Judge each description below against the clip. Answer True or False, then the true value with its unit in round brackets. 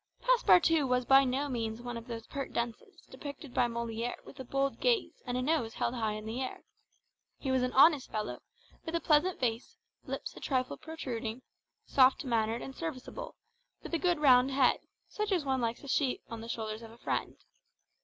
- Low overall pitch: False (255 Hz)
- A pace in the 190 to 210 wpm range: True (195 wpm)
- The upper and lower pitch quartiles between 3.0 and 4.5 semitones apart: True (3.9 semitones)